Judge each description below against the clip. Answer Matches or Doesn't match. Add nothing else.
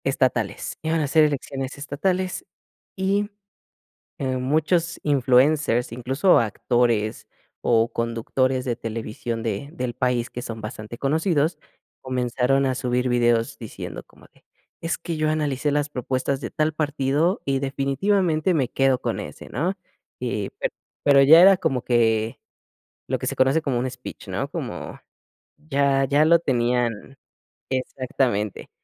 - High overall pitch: Doesn't match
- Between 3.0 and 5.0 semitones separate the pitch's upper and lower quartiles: Matches